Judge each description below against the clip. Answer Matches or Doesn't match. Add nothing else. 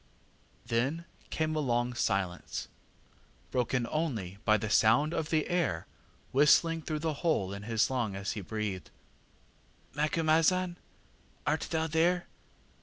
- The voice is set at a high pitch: Doesn't match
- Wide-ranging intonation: Matches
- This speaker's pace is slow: Matches